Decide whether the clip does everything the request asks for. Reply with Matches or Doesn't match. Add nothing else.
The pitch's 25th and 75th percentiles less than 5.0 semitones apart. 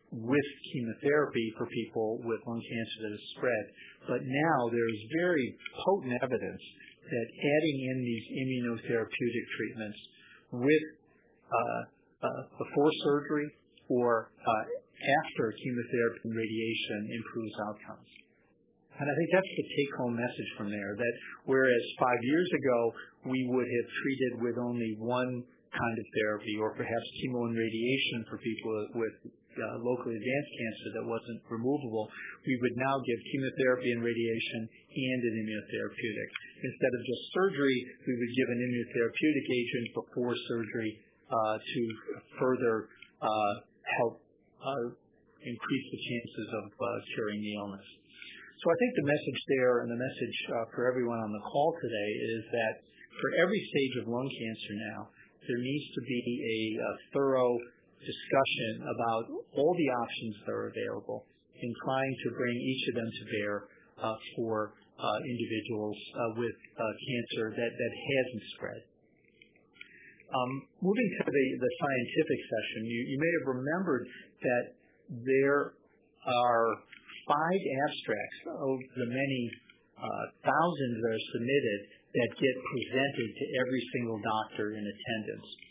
Matches